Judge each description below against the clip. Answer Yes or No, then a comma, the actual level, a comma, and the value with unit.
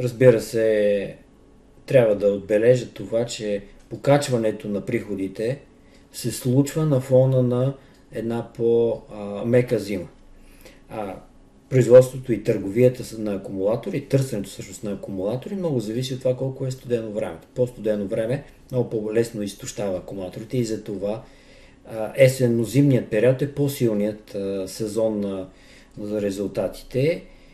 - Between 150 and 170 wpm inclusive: No, average, 120 wpm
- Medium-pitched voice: No, low, 115 Hz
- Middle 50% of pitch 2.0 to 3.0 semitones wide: No, average, 3.4 semitones